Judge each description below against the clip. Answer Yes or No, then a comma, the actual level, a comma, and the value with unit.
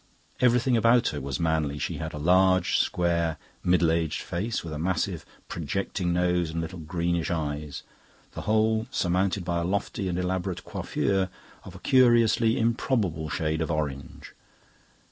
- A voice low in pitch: Yes, very low, 90 Hz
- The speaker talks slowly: No, average, 150 wpm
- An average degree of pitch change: Yes, average, 3.7 semitones